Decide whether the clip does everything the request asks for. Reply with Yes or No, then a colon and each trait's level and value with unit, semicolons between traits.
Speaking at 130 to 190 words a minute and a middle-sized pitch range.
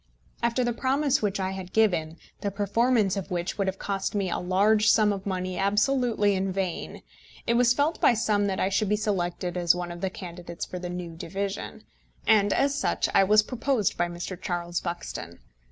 No: average, 200 wpm; average, 3.2 semitones